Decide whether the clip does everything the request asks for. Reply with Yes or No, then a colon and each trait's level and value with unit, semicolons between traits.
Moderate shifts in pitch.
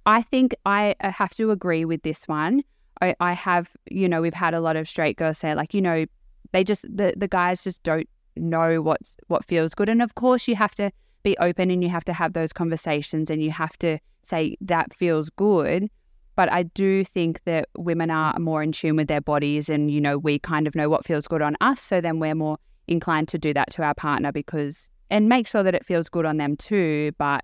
Yes: average, 3.6 semitones